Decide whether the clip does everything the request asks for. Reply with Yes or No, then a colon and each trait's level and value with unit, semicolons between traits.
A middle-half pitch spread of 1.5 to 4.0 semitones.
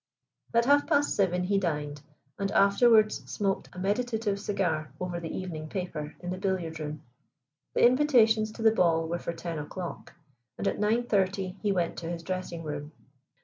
No: average, 4.4 semitones